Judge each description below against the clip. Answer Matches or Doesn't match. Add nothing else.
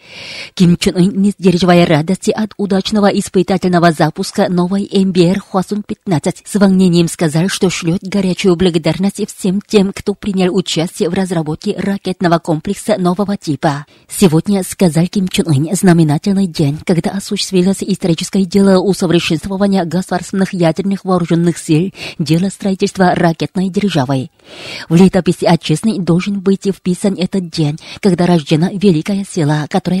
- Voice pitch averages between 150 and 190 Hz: Matches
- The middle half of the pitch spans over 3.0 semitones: Doesn't match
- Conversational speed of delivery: Matches